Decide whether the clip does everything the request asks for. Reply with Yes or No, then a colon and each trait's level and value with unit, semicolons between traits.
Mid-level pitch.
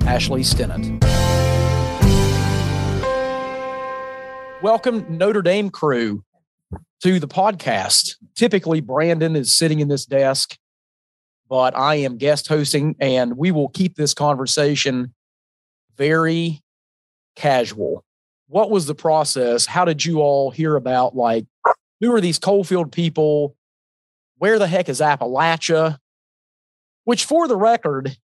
Yes: medium, 150 Hz